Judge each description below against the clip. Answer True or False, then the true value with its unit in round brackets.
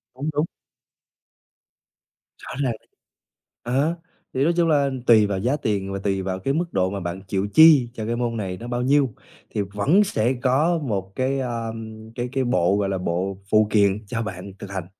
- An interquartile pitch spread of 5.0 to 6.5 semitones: True (5.6 semitones)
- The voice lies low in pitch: True (115 Hz)